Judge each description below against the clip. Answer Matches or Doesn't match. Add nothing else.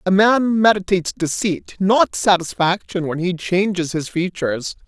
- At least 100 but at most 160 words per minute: Matches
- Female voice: Doesn't match